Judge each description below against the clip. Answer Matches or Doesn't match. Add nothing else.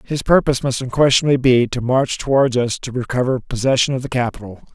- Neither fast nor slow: Matches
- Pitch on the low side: Matches